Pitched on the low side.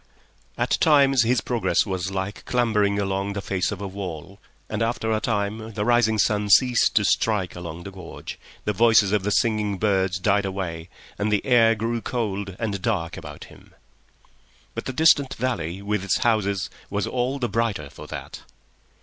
Yes: low, 105 Hz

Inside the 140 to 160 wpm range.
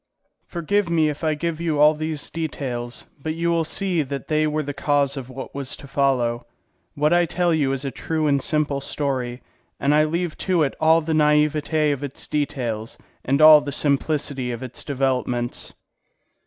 No: average, 185 wpm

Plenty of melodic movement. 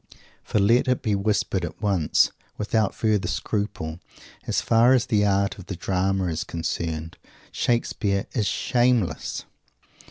No: average, 3.7 semitones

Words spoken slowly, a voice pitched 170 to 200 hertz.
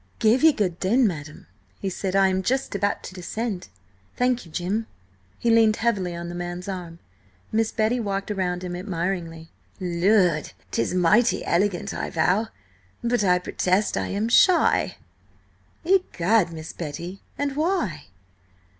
No: average, 145 wpm; high, 190 Hz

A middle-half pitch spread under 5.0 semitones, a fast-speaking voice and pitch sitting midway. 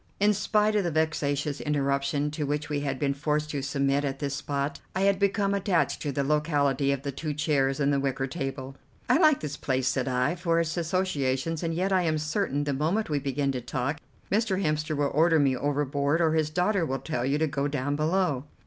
Yes: average, 3.1 semitones; fast, 220 wpm; medium, 145 Hz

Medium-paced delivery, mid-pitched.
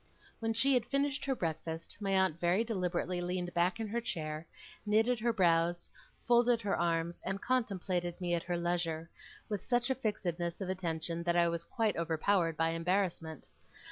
Yes: average, 170 wpm; medium, 180 Hz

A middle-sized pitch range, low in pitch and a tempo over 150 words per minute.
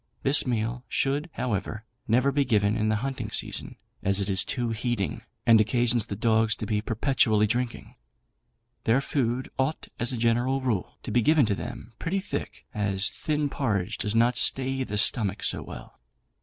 Yes: average, 3.5 semitones; low, 115 Hz; average, 175 wpm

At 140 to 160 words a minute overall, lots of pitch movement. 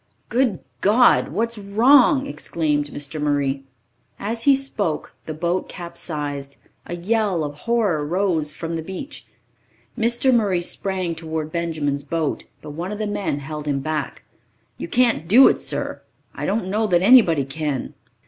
Yes: average, 155 wpm; wide, 6.3 semitones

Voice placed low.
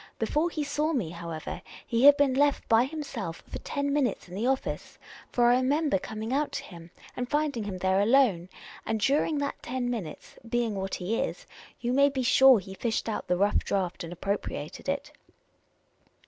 No: high, 240 Hz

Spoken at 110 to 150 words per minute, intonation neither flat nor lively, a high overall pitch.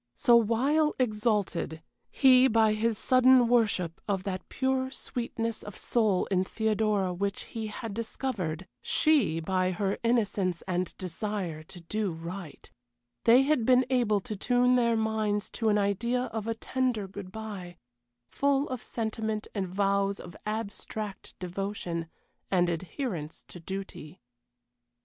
Yes: slow, 135 wpm; average, 4.0 semitones; high, 210 Hz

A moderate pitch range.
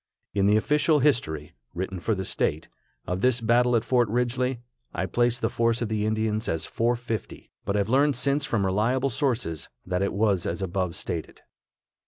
Yes: average, 4.4 semitones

